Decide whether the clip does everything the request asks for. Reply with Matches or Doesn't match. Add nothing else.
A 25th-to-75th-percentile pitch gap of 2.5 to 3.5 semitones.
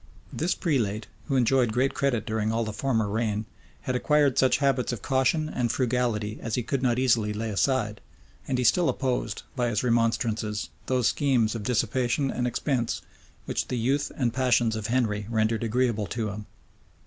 Matches